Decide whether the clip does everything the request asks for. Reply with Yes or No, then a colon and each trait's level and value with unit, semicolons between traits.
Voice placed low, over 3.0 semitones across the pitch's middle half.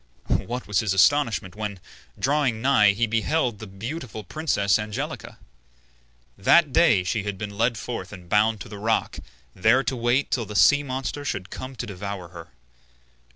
Yes: low, 110 Hz; average, 4.1 semitones